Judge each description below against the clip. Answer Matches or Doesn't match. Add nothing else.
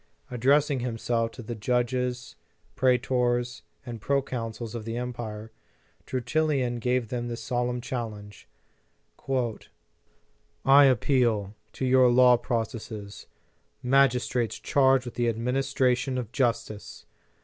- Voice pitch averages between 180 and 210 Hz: Doesn't match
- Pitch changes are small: Matches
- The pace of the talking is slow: Matches